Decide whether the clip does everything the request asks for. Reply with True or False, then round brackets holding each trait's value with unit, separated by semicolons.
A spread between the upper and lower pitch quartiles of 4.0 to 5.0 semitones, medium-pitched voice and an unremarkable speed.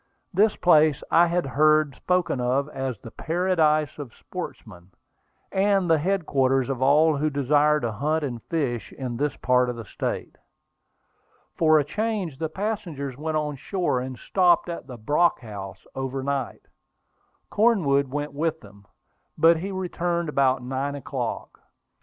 True (4.4 semitones; 150 Hz; 150 wpm)